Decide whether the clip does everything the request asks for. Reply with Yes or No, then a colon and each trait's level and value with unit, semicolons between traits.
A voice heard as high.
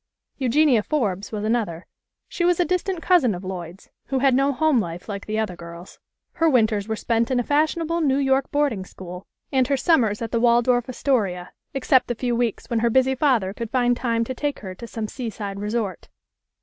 Yes: high, 235 Hz